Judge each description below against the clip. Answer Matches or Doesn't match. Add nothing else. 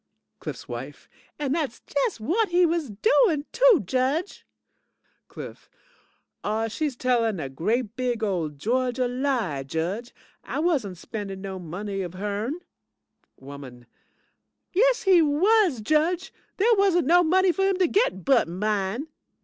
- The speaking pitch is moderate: Doesn't match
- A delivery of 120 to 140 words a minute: Matches